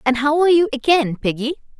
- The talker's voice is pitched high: Yes, very high, 285 Hz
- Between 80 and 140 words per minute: No, average, 200 wpm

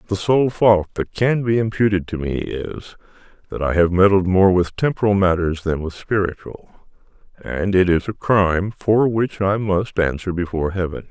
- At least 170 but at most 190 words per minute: Yes, average, 180 wpm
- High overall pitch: No, very low, 95 Hz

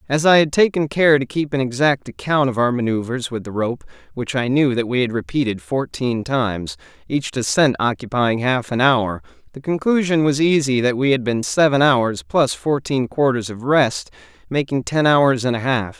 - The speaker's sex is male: Yes, male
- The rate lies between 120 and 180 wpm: No, average, 195 wpm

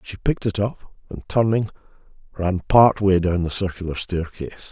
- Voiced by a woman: No, male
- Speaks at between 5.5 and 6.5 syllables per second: Yes, 5.7 syllables/s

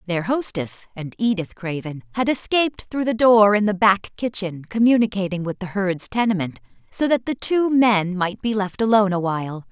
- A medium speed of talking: Yes, average, 185 wpm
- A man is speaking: No, female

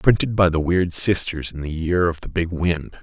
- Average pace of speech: No, fast, 240 wpm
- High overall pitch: No, very low, 85 Hz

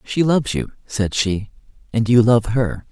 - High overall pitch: No, low, 115 Hz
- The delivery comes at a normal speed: Yes, average, 185 wpm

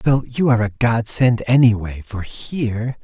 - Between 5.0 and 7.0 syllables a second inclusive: No, 4.7 syllables/s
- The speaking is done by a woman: No, male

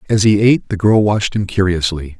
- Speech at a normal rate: No, fast, 220 wpm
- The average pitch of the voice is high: No, low, 100 Hz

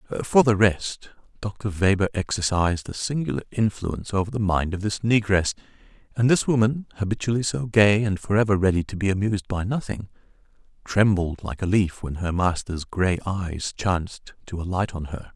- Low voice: Yes, low, 100 Hz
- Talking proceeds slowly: No, average, 170 wpm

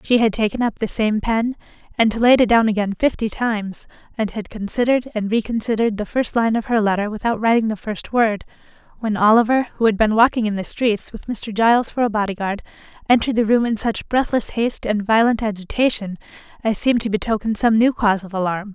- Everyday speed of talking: No, fast, 210 wpm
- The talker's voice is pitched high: Yes, high, 220 Hz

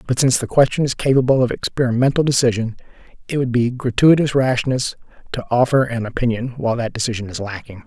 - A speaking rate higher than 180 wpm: No, average, 175 wpm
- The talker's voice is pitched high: No, low, 125 Hz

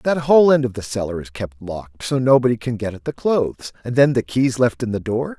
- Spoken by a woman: No, male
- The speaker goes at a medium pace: No, fast, 270 wpm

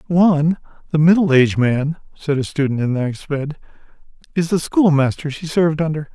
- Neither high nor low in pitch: Yes, medium, 155 Hz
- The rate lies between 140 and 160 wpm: Yes, average, 155 wpm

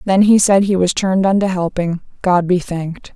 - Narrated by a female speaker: Yes, female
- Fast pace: Yes, fast, 210 wpm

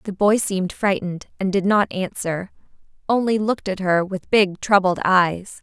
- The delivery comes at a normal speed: Yes, average, 170 wpm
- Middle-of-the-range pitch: No, high, 195 Hz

